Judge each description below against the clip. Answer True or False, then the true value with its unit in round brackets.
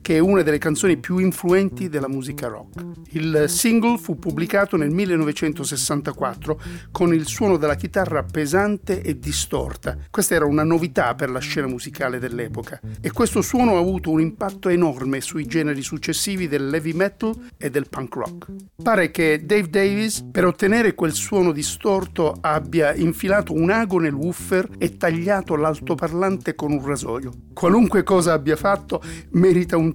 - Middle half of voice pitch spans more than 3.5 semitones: True (4.2 semitones)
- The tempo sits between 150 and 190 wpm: True (155 wpm)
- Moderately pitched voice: True (165 Hz)